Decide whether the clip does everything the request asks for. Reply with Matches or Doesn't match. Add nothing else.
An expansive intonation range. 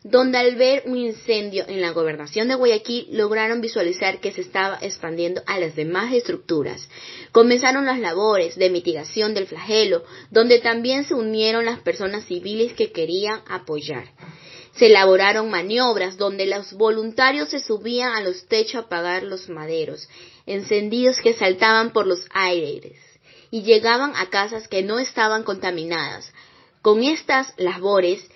Doesn't match